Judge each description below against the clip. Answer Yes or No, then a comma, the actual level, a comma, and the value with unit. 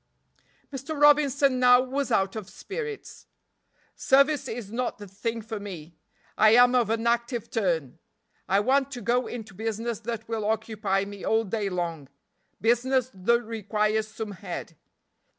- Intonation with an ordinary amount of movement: Yes, average, 3.5 semitones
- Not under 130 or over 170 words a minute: Yes, average, 150 wpm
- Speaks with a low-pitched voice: No, high, 225 Hz